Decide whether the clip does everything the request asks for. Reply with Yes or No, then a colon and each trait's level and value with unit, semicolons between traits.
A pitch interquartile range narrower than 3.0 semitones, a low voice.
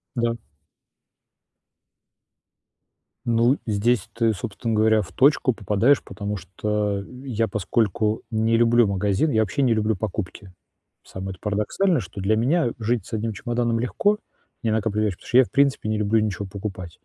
Yes: narrow, 2.6 semitones; low, 110 Hz